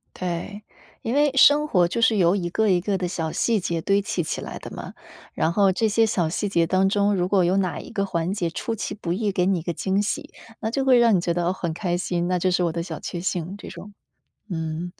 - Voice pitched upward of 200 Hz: No, medium, 185 Hz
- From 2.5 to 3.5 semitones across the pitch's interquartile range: Yes, average, 3.1 semitones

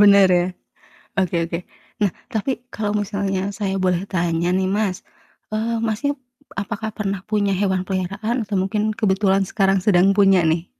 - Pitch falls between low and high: No, high, 195 Hz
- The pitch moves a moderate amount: No, narrow, 2.0 semitones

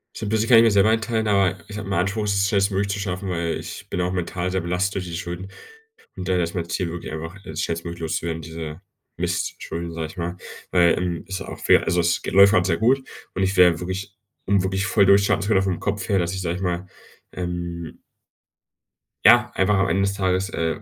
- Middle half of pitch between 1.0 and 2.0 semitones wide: No, narrow, 2.4 semitones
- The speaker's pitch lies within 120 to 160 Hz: No, very low, 95 Hz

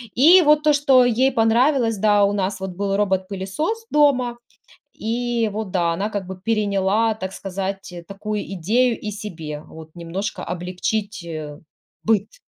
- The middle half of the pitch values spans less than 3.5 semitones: No, average, 4.0 semitones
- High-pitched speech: Yes, high, 205 Hz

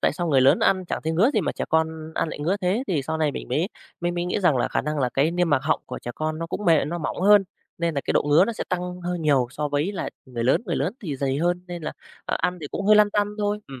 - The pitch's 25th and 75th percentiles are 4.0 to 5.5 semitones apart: No, average, 3.6 semitones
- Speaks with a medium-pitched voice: Yes, medium, 165 Hz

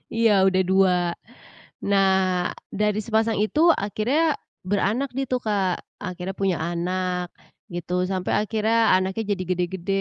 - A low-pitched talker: No, high, 195 Hz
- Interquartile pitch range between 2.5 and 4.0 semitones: Yes, average, 2.8 semitones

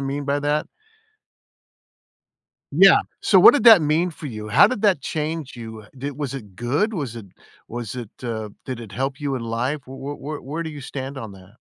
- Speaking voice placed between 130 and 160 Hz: Yes, low, 135 Hz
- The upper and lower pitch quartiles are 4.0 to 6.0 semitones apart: Yes, average, 4.4 semitones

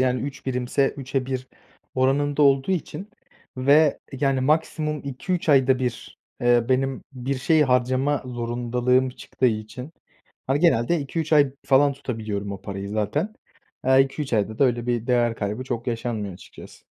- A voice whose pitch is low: Yes, low, 130 Hz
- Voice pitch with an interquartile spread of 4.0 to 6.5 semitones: No, average, 2.7 semitones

